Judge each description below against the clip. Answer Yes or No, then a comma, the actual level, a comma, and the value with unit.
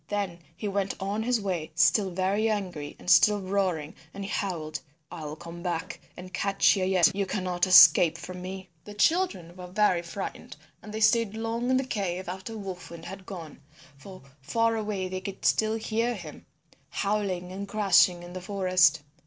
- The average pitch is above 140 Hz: Yes, high, 190 Hz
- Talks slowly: No, average, 185 wpm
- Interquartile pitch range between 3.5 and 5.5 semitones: No, average, 2.8 semitones